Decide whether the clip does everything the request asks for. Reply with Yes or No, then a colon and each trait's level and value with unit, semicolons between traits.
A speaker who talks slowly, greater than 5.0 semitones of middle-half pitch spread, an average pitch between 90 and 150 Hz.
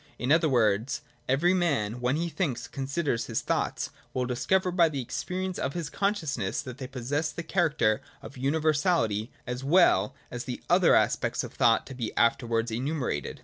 No: average, 175 wpm; wide, 5.4 semitones; low, 135 Hz